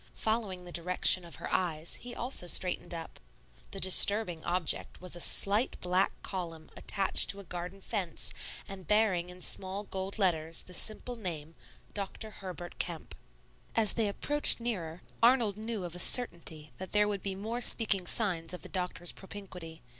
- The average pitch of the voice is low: No, medium, 185 Hz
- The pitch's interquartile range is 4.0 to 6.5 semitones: No, average, 3.1 semitones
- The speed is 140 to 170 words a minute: Yes, average, 165 wpm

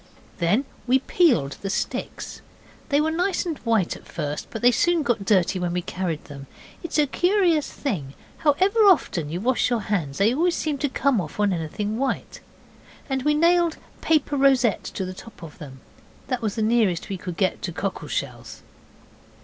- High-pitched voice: Yes, high, 230 Hz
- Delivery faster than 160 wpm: Yes, average, 190 wpm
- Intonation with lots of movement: Yes, wide, 8.4 semitones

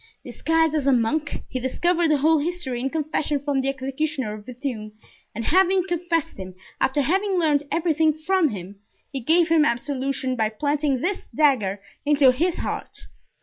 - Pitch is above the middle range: Yes, very high, 290 Hz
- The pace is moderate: Yes, average, 165 wpm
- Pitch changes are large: No, average, 4.0 semitones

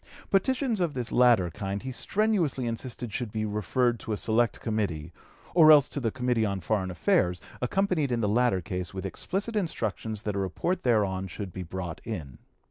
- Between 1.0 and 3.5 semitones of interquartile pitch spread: No, average, 5.3 semitones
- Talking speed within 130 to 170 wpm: No, average, 185 wpm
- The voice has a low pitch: Yes, low, 110 Hz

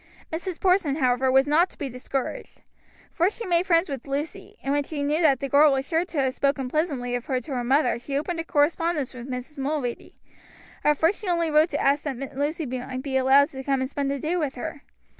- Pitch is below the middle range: No, very high, 285 Hz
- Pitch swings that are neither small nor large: Yes, average, 3.3 semitones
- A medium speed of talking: No, fast, 235 wpm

